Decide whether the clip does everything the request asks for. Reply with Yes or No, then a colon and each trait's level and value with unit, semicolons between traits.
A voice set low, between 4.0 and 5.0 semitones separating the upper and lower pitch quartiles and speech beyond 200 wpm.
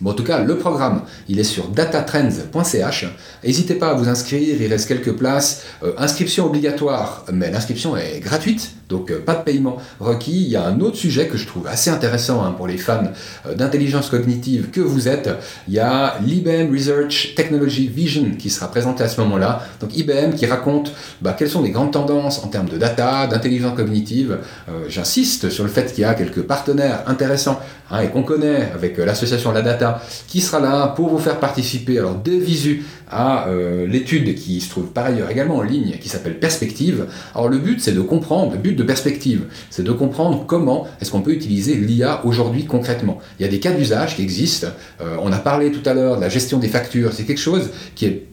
Yes: low, 130 Hz; average, 4.6 semitones; average, 215 wpm